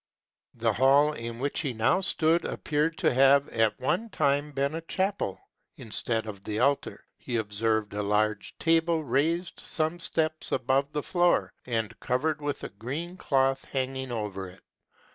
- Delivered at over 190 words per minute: No, average, 160 wpm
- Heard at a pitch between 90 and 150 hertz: Yes, low, 135 Hz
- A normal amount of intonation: No, wide, 5.7 semitones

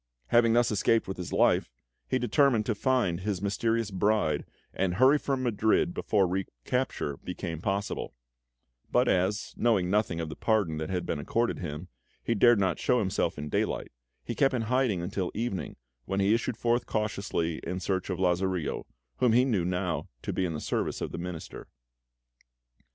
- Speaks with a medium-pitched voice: No, low, 100 Hz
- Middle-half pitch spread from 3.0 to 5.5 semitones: Yes, average, 4.6 semitones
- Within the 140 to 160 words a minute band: No, average, 175 wpm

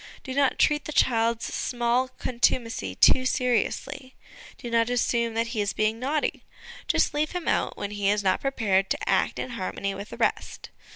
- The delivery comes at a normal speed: Yes, average, 180 wpm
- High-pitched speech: Yes, high, 235 Hz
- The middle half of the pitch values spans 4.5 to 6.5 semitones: No, average, 3.3 semitones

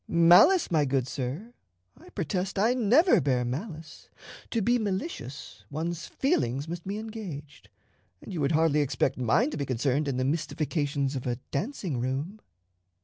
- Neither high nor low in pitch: Yes, medium, 160 Hz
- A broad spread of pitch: Yes, wide, 6.7 semitones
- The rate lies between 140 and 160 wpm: Yes, average, 155 wpm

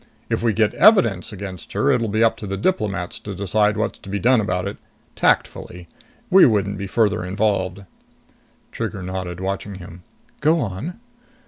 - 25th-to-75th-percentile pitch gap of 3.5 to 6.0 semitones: No, average, 3.1 semitones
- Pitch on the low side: Yes, low, 100 Hz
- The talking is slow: No, average, 165 wpm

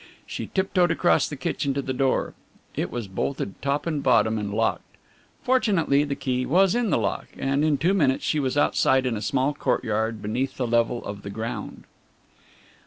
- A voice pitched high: No, low, 135 Hz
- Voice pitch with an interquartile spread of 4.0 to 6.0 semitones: Yes, average, 4.6 semitones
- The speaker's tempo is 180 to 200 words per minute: Yes, average, 185 wpm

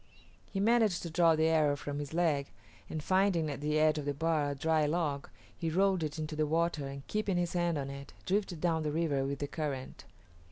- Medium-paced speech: No, fast, 225 wpm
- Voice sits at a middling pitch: Yes, medium, 155 Hz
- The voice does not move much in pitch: No, average, 3.1 semitones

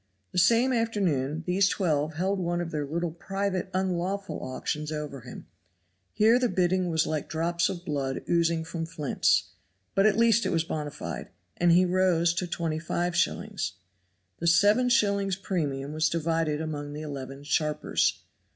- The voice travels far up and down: No, average, 3.6 semitones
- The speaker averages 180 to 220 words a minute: No, average, 155 wpm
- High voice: No, medium, 170 Hz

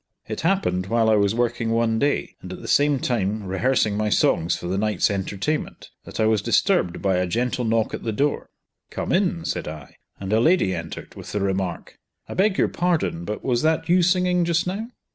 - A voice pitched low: Yes, low, 110 Hz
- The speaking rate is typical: No, fast, 210 wpm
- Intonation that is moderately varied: No, wide, 8.1 semitones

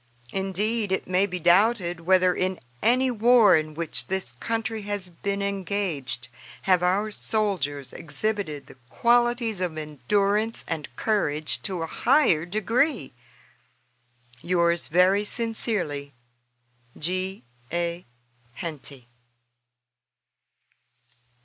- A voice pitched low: No, medium, 185 Hz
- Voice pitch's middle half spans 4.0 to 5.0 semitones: Yes, average, 4.5 semitones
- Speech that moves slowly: Yes, slow, 100 wpm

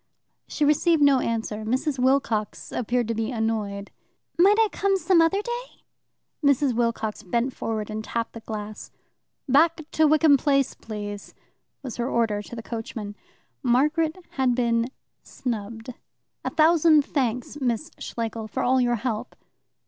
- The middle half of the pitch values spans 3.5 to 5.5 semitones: Yes, average, 4.9 semitones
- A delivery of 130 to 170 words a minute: Yes, average, 145 wpm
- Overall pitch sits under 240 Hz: No, high, 245 Hz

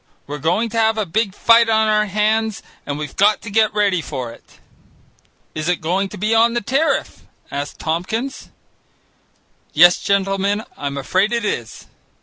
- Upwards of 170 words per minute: No, average, 165 wpm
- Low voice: No, high, 205 Hz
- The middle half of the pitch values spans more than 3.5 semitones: Yes, average, 5.2 semitones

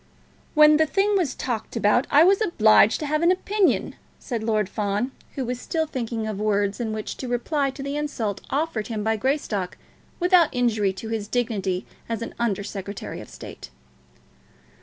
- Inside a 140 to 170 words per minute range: No, average, 180 wpm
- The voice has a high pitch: Yes, high, 235 Hz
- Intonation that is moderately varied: No, wide, 5.9 semitones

